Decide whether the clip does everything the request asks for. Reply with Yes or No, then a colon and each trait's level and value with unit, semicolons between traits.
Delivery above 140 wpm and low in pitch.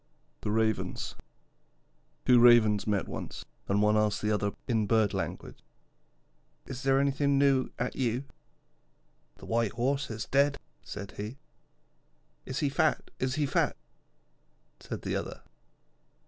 No: slow, 135 wpm; low, 120 Hz